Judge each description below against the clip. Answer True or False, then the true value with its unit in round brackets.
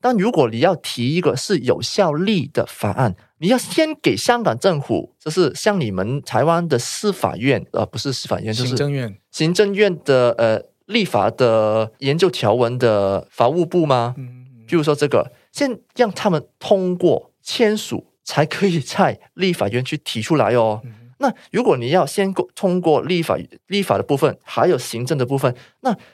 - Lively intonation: True (7.5 semitones)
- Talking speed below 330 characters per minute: True (255 characters per minute)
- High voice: False (145 Hz)